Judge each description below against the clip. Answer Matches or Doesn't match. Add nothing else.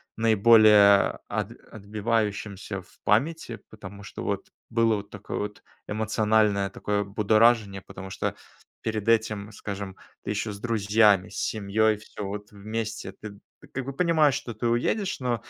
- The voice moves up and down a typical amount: Doesn't match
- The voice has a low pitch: Matches